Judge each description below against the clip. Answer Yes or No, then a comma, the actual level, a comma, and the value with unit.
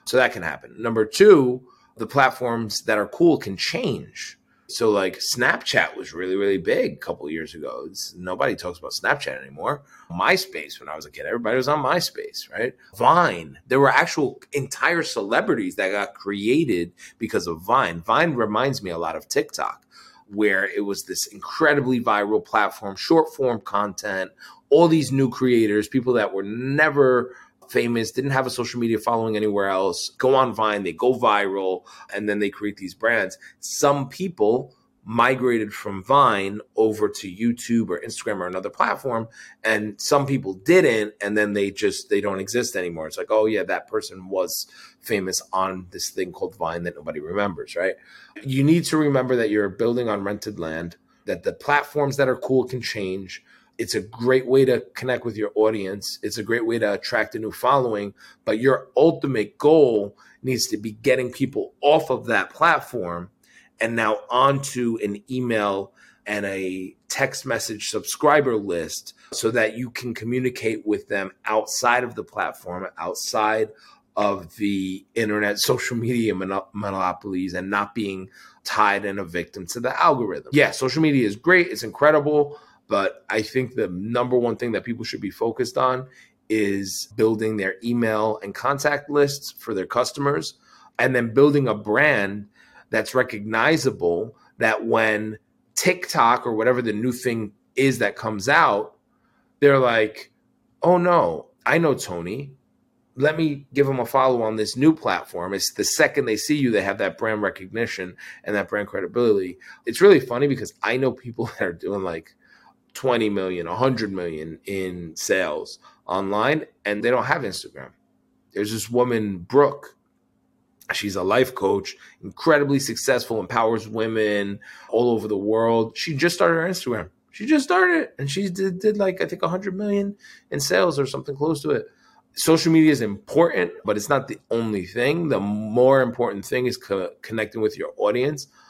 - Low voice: Yes, low, 115 Hz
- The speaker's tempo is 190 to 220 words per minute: No, average, 170 wpm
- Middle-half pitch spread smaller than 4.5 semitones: No, average, 5.0 semitones